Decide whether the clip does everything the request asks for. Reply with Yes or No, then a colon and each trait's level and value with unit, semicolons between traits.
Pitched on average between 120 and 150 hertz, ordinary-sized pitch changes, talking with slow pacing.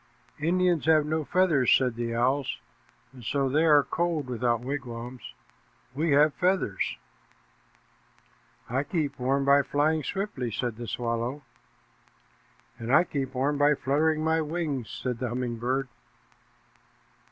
Yes: medium, 140 Hz; average, 3.9 semitones; slow, 130 wpm